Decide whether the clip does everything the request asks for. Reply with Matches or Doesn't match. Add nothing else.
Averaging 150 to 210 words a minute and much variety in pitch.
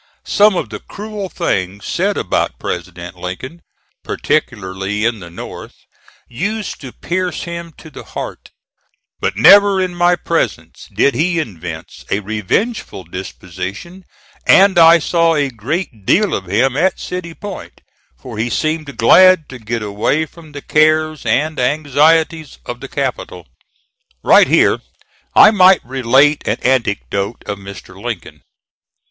Doesn't match